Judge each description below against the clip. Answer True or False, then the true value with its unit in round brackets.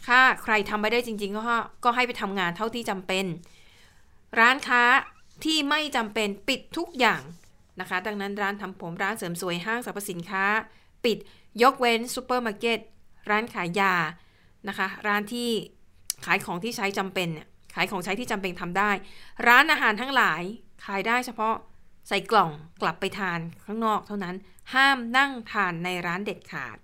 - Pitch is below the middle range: False (205 Hz)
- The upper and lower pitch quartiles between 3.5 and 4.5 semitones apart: True (4.2 semitones)